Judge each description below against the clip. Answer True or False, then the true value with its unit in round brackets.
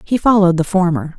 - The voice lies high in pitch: False (180 Hz)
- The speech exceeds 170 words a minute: True (200 wpm)